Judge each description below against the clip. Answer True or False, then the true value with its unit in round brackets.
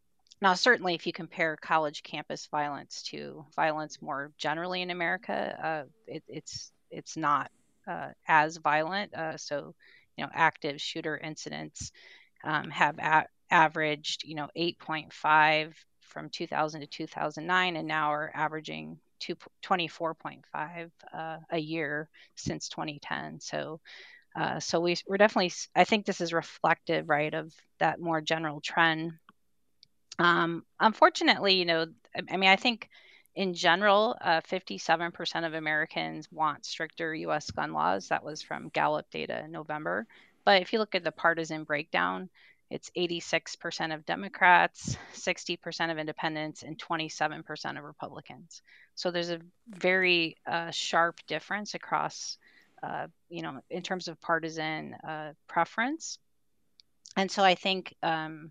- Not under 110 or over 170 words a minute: True (140 wpm)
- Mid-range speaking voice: True (165 Hz)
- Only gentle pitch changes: True (2.3 semitones)